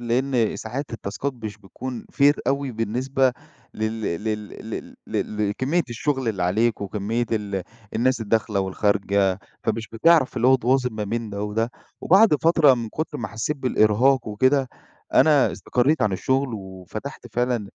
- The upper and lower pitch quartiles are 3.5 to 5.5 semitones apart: Yes, average, 3.9 semitones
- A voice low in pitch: Yes, low, 115 Hz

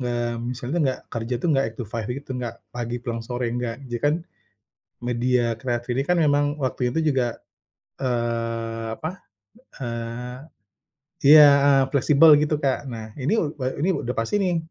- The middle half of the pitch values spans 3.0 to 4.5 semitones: Yes, average, 3.4 semitones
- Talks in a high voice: No, low, 125 Hz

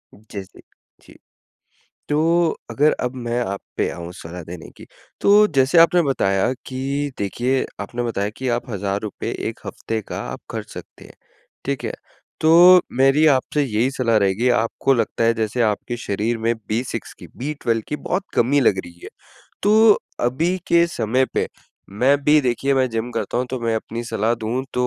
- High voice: No, low, 125 Hz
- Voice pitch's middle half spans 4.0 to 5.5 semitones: Yes, average, 4.3 semitones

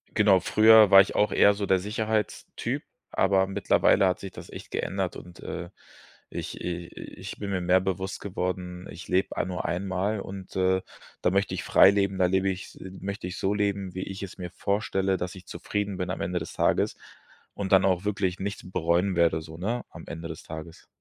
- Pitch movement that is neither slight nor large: No, narrow, 1.8 semitones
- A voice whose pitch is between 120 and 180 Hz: No, very low, 95 Hz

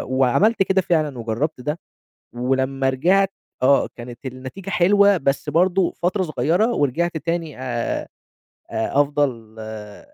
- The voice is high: No, medium, 145 Hz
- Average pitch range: No, wide, 5.7 semitones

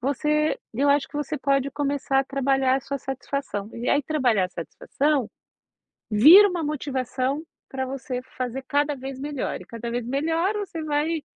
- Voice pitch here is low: No, very high, 275 Hz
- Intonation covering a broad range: No, narrow, 2.4 semitones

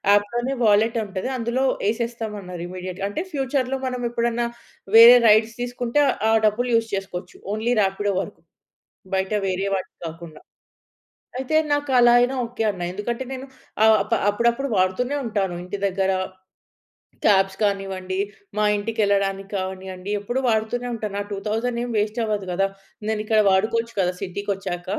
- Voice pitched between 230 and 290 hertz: No, high, 210 Hz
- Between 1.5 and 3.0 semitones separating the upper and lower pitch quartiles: No, average, 3.6 semitones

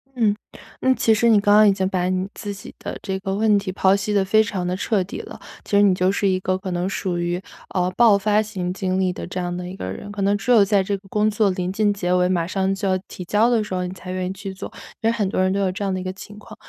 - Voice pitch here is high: Yes, high, 195 Hz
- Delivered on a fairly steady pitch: Yes, narrow, 2.0 semitones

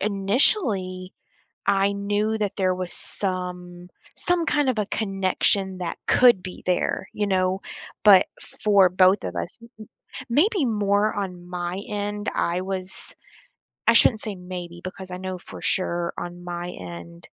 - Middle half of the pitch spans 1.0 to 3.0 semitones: Yes, narrow, 2.4 semitones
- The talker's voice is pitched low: No, high, 190 Hz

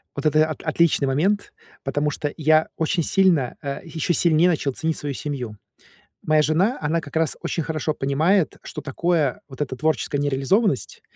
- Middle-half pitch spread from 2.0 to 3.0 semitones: Yes, average, 2.7 semitones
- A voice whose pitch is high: No, medium, 155 Hz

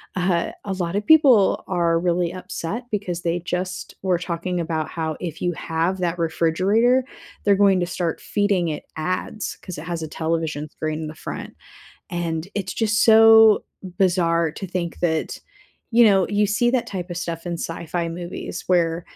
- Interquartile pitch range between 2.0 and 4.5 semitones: Yes, average, 2.8 semitones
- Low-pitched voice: No, medium, 175 Hz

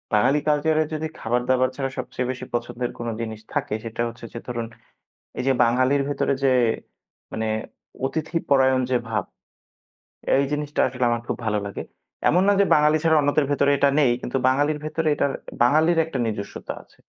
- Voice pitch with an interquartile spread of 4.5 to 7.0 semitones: No, average, 3.7 semitones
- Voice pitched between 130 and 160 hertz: Yes, low, 135 Hz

